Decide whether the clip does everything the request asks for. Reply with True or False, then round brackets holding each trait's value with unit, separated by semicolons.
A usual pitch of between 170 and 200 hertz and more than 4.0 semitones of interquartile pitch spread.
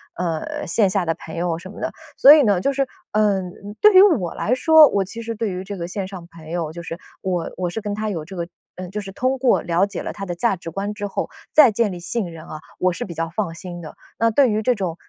True (195 Hz; 4.4 semitones)